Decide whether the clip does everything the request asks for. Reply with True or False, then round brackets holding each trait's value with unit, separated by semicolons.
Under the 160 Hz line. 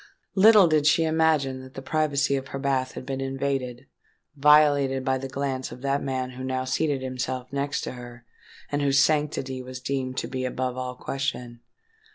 True (135 Hz)